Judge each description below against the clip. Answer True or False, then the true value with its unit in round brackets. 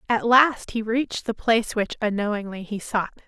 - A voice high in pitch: True (220 Hz)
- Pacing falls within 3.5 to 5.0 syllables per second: False (5.2 syllables/s)